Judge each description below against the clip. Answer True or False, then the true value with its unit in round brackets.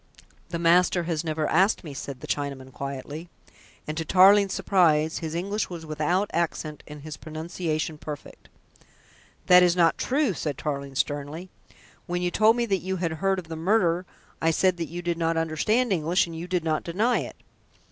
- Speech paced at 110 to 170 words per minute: False (185 wpm)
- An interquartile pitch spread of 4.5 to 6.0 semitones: False (2.9 semitones)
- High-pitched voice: False (165 Hz)